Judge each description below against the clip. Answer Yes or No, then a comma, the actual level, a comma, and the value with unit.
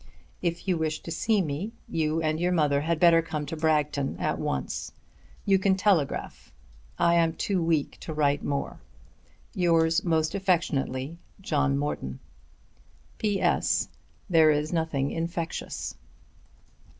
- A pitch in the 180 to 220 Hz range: No, medium, 160 Hz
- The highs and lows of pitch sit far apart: No, narrow, 2.6 semitones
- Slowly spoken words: Yes, slow, 125 wpm